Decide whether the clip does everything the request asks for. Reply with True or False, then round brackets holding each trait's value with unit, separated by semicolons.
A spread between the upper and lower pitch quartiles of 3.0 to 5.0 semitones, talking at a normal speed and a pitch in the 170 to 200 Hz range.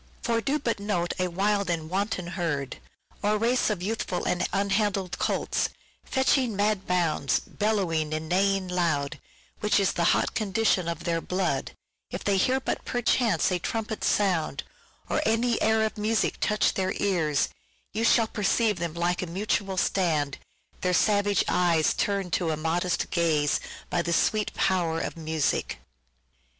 True (3.8 semitones; 160 wpm; 190 Hz)